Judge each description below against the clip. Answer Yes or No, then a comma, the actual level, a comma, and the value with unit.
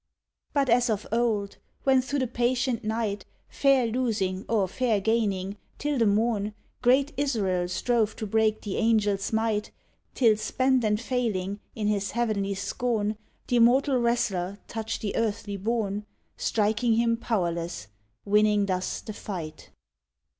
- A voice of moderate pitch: No, high, 220 Hz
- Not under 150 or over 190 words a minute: No, average, 140 wpm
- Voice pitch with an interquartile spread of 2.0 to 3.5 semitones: Yes, average, 2.9 semitones